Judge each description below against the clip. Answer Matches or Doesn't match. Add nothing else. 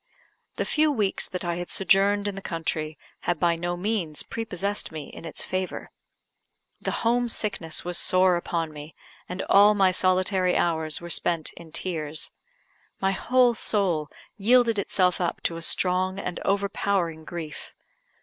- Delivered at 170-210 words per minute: Doesn't match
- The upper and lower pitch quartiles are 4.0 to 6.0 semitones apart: Doesn't match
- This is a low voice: Doesn't match